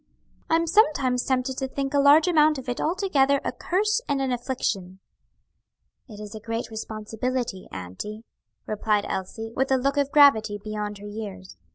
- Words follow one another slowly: No, average, 165 wpm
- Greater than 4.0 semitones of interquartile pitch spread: Yes, average, 5.0 semitones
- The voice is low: No, very high, 250 Hz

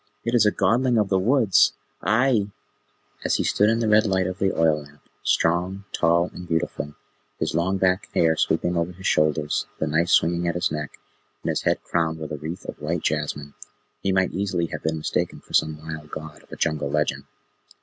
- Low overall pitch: Yes, very low, 85 Hz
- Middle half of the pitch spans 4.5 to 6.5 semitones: No, average, 3.8 semitones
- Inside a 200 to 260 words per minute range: Yes, fast, 205 wpm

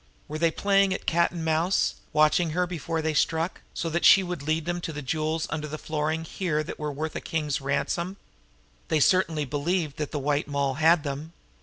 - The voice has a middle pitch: Yes, medium, 160 Hz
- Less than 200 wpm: No, fast, 205 wpm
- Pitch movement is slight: Yes, narrow, 2.3 semitones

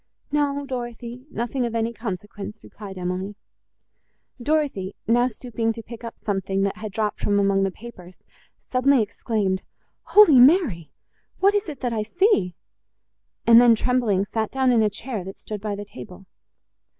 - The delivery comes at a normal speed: Yes, average, 155 wpm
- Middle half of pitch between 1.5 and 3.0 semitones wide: No, average, 4.1 semitones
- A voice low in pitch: No, high, 225 Hz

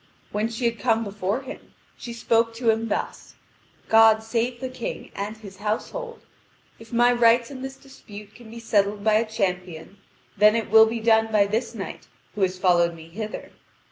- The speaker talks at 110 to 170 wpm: No, average, 185 wpm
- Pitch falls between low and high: No, high, 220 Hz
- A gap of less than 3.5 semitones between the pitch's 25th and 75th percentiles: Yes, narrow, 2.4 semitones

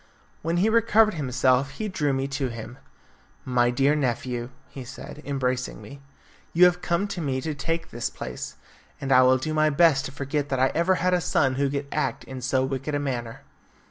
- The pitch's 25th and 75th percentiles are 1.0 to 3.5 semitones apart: No, average, 3.9 semitones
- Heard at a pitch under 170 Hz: Yes, medium, 140 Hz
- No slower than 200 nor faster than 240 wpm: Yes, fast, 205 wpm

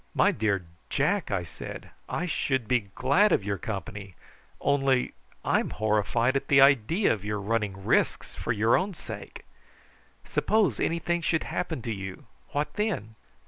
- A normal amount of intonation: No, wide, 7.3 semitones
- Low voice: Yes, low, 120 Hz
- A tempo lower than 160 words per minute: Yes, average, 150 wpm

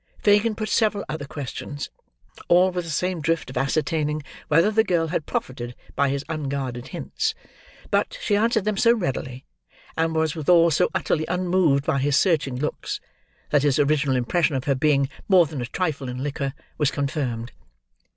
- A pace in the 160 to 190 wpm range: Yes, average, 170 wpm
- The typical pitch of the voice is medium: Yes, medium, 155 Hz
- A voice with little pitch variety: No, average, 4.5 semitones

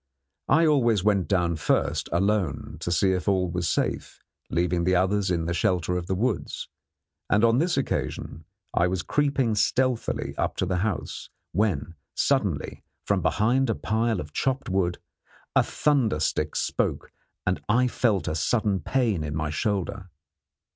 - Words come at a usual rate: Yes, average, 160 wpm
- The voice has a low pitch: Yes, very low, 95 Hz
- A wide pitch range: No, average, 4.7 semitones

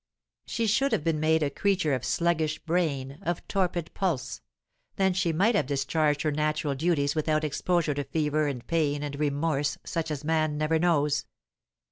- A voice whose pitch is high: No, medium, 155 Hz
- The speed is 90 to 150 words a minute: No, average, 170 wpm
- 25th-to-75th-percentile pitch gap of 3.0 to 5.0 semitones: No, narrow, 2.6 semitones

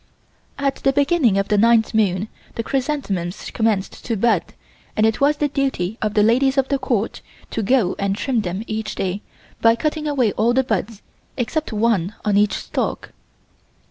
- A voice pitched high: Yes, high, 225 Hz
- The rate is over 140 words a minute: Yes, average, 175 wpm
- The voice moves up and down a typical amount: Yes, average, 4.6 semitones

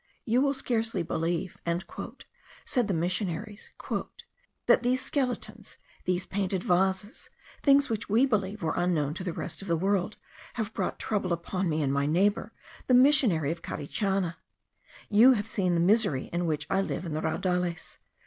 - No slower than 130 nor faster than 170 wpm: Yes, average, 160 wpm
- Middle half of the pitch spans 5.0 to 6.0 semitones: No, average, 4.6 semitones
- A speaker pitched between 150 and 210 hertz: Yes, high, 190 Hz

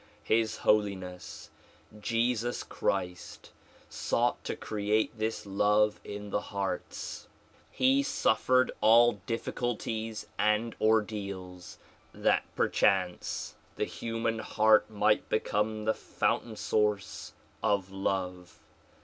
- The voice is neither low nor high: No, low, 105 Hz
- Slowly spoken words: Yes, slow, 95 wpm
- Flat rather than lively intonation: Yes, narrow, 2.2 semitones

